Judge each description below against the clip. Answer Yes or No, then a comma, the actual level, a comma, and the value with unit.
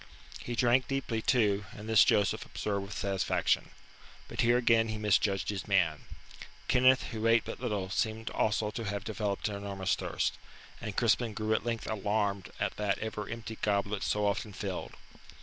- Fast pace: No, average, 170 wpm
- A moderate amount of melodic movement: No, narrow, 2.1 semitones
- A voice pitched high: No, low, 105 Hz